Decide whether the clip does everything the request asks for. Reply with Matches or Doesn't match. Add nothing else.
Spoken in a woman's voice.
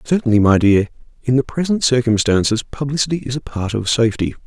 Doesn't match